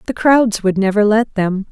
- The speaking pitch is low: No, high, 210 Hz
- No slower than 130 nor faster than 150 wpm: No, fast, 210 wpm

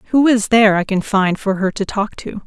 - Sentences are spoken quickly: Yes, fast, 270 wpm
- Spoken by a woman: Yes, female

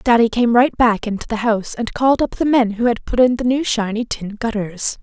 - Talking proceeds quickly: Yes, fast, 250 wpm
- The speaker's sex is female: Yes, female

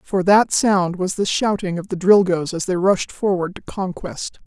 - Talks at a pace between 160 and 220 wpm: Yes, average, 200 wpm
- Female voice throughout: Yes, female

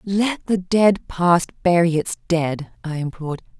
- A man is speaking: No, female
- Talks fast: No, average, 150 wpm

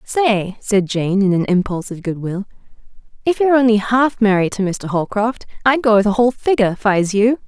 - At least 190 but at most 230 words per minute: Yes, average, 195 wpm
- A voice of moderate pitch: No, high, 215 Hz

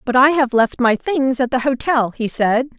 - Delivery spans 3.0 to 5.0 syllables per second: Yes, 4.6 syllables/s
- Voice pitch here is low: No, very high, 255 Hz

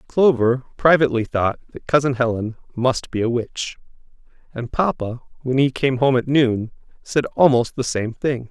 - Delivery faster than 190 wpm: No, average, 160 wpm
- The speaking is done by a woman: No, male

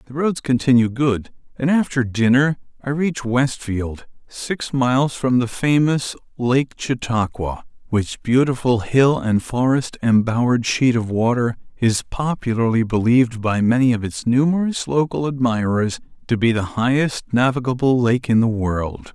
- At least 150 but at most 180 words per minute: No, average, 140 wpm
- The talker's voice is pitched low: Yes, low, 125 Hz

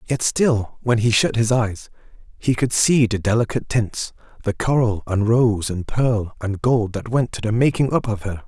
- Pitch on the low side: Yes, low, 115 Hz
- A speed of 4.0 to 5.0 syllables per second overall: Yes, 4.6 syllables/s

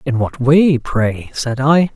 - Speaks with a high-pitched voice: No, low, 135 Hz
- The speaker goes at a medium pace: Yes, average, 185 wpm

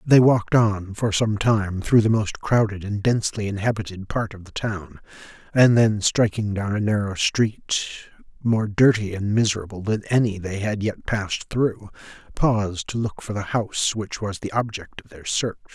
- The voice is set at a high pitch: No, low, 105 Hz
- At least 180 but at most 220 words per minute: Yes, average, 185 wpm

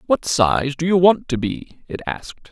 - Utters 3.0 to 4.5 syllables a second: Yes, 4.4 syllables/s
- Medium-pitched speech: Yes, medium, 145 Hz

